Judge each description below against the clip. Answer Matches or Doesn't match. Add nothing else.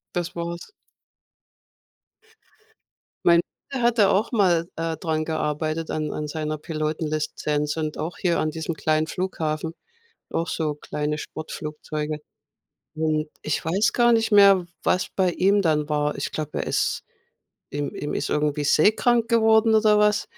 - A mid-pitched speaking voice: Matches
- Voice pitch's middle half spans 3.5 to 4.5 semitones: Matches